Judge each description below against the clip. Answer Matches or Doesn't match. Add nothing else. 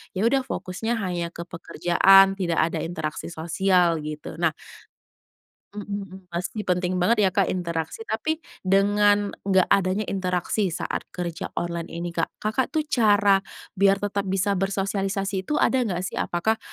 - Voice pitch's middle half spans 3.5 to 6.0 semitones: Doesn't match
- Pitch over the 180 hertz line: Matches